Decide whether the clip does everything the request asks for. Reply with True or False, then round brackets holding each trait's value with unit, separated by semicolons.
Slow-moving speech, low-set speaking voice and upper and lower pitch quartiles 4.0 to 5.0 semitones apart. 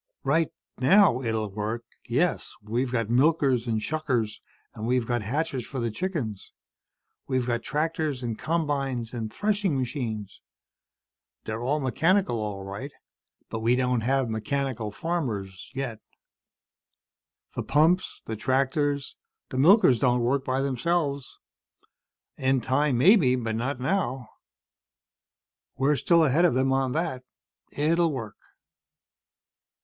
True (125 wpm; 130 Hz; 4.3 semitones)